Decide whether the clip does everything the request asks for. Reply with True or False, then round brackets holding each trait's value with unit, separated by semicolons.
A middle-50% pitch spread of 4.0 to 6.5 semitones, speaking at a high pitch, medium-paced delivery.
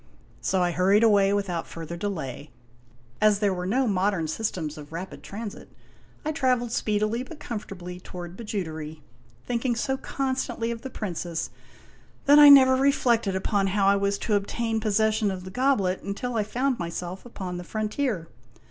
True (4.5 semitones; 205 Hz; 165 wpm)